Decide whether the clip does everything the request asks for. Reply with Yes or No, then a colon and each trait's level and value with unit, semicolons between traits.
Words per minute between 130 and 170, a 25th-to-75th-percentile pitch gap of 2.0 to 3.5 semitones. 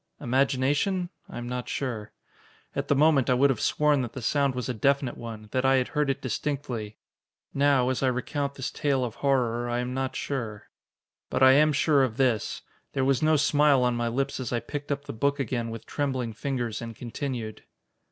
No: fast, 205 wpm; average, 2.8 semitones